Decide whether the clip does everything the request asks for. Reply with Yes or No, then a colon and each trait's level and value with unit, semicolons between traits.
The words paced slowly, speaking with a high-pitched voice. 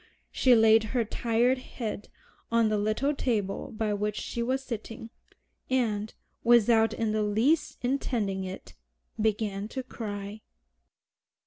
Yes: slow, 125 wpm; high, 225 Hz